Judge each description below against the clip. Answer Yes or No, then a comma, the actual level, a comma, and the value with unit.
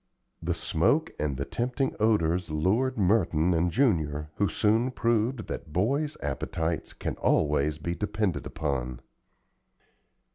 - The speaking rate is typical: No, slow, 120 wpm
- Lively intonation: Yes, wide, 6.6 semitones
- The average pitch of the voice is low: Yes, very low, 90 Hz